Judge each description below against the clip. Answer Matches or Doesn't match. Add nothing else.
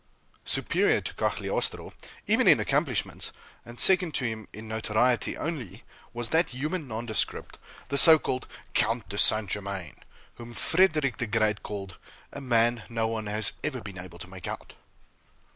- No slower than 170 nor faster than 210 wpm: Doesn't match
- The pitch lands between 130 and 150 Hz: Doesn't match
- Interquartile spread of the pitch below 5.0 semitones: Matches